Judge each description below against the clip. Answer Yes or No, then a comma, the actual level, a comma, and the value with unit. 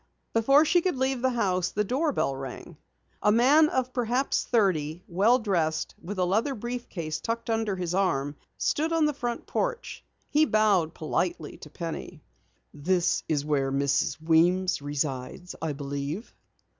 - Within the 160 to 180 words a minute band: No, average, 150 wpm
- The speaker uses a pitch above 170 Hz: Yes, high, 190 Hz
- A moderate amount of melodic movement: No, wide, 7.6 semitones